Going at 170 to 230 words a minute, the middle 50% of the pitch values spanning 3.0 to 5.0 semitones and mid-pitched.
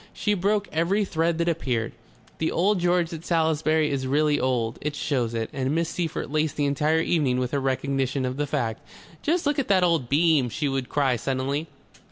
Yes: average, 200 wpm; average, 4.1 semitones; medium, 150 Hz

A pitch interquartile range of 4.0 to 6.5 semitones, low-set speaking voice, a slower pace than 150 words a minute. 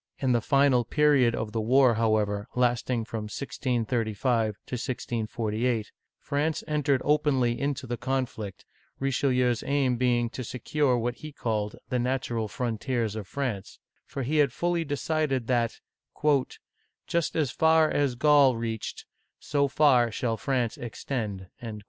No: average, 3.5 semitones; low, 125 Hz; average, 140 wpm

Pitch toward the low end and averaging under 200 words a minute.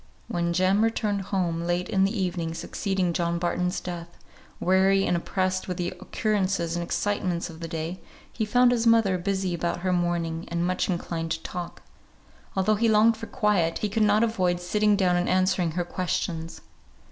No: medium, 185 Hz; average, 180 wpm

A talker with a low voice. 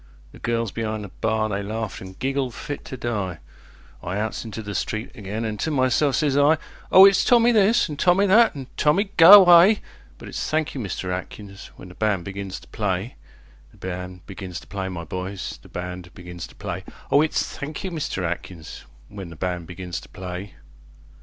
Yes: low, 105 Hz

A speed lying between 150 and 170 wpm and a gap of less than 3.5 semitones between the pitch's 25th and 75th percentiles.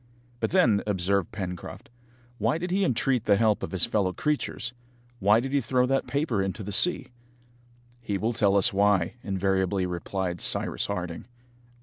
No: average, 160 wpm; average, 4.7 semitones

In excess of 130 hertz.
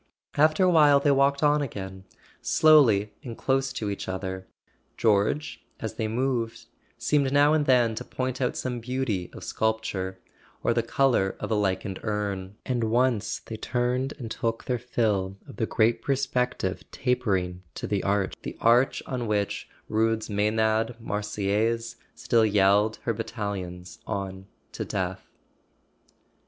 No: low, 110 Hz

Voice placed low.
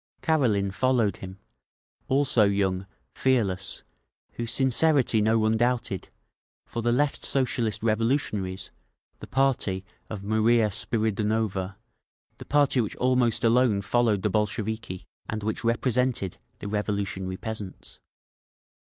Yes: low, 110 Hz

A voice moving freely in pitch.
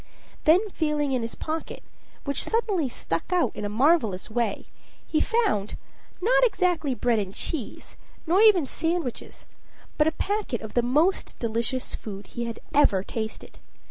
Yes: wide, 7.4 semitones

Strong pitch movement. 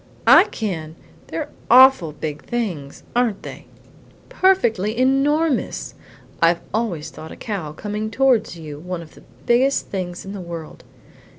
Yes: wide, 6.7 semitones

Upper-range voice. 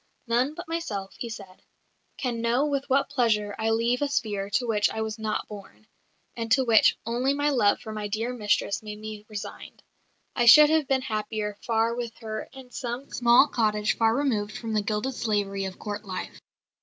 Yes: high, 225 Hz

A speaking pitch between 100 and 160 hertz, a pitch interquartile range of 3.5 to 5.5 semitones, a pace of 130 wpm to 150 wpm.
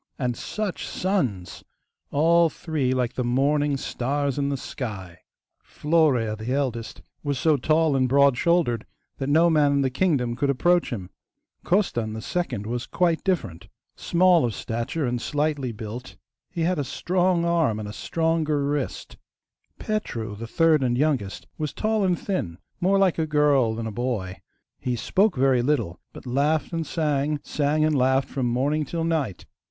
No: medium, 140 Hz; average, 5.1 semitones; average, 165 wpm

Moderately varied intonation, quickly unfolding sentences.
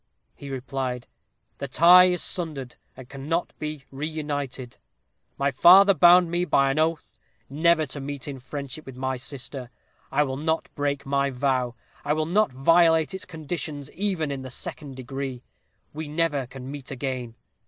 No: average, 3.3 semitones; average, 160 wpm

